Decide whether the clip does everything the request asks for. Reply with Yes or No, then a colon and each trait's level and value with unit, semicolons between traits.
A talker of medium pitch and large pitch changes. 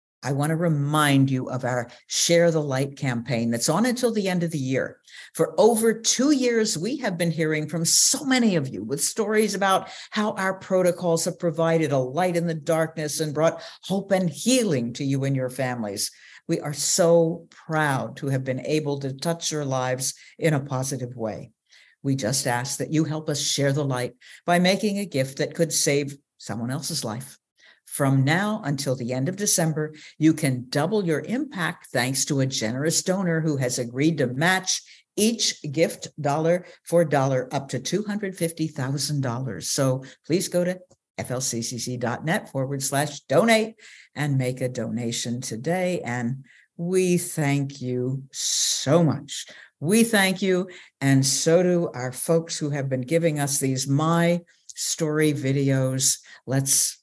No: medium, 150 Hz; average, 4.7 semitones